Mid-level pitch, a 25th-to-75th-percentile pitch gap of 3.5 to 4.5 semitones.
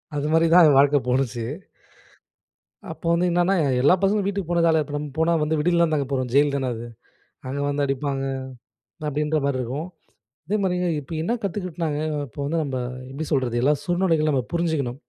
Yes: medium, 150 Hz; average, 3.8 semitones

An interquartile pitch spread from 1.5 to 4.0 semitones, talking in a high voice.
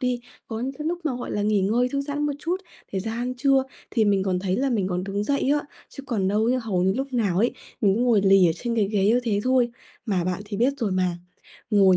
No: average, 4.5 semitones; high, 220 Hz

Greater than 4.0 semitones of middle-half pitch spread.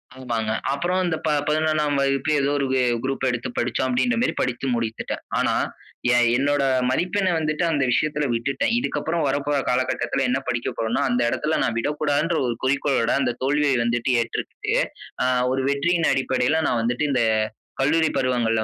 No: average, 3.7 semitones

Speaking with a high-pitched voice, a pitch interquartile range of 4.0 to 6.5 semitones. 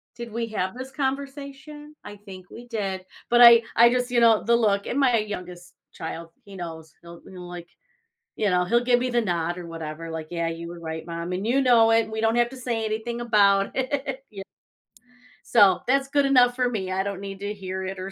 Yes: high, 215 Hz; average, 5.0 semitones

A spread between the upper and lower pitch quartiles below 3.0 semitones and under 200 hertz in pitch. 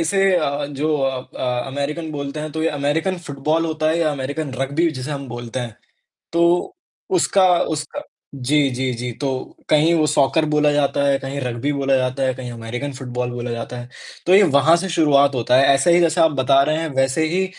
No: average, 3.3 semitones; medium, 140 Hz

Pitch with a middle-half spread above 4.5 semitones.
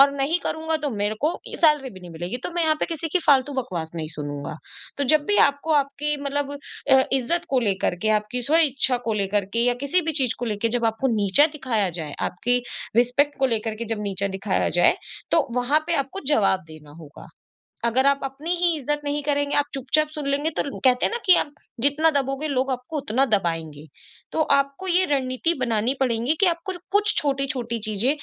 Yes: average, 5.0 semitones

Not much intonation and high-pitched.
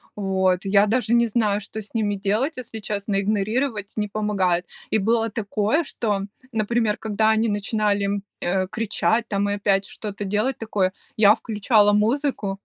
Yes: narrow, 2.0 semitones; high, 210 Hz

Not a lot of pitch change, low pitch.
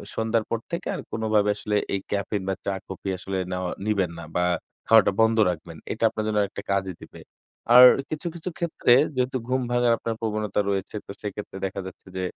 No: average, 3.0 semitones; low, 105 Hz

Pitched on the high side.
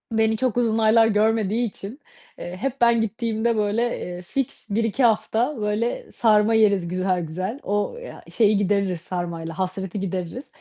Yes: high, 215 Hz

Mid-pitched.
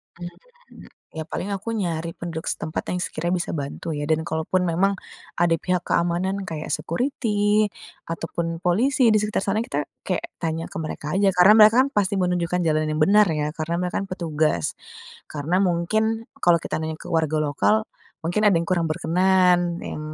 Yes: medium, 175 Hz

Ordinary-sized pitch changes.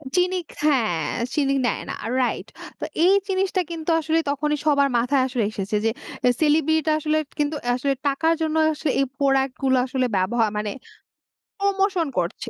Yes: average, 3.7 semitones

